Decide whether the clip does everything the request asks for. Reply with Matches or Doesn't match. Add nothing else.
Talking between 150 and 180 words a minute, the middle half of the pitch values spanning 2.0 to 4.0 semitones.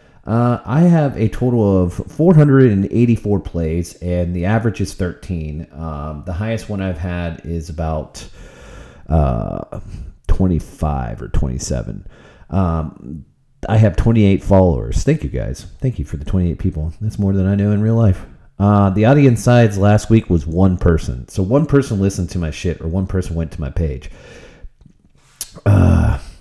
Doesn't match